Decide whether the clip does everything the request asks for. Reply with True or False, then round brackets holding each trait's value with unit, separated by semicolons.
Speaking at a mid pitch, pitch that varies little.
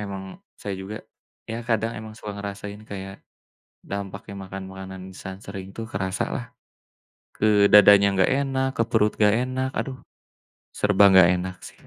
False (100 Hz; 2.3 semitones)